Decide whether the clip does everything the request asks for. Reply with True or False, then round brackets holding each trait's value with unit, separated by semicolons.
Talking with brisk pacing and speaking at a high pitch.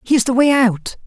True (225 wpm; 245 Hz)